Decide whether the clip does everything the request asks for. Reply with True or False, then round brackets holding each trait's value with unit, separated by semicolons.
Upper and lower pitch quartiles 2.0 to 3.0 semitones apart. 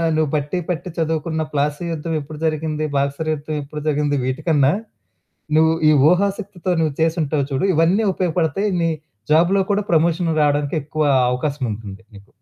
True (2.6 semitones)